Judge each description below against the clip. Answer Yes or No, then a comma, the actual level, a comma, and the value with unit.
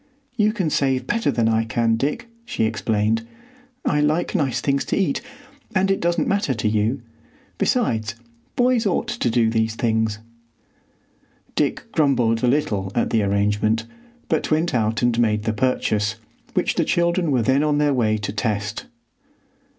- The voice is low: Yes, low, 120 Hz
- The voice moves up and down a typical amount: No, wide, 5.8 semitones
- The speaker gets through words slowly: No, average, 160 wpm